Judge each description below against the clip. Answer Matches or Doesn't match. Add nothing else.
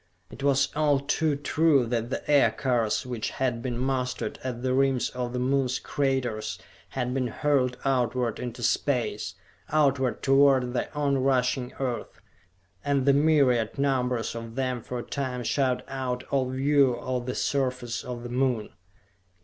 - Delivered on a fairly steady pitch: Matches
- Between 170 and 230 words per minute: Doesn't match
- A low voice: Matches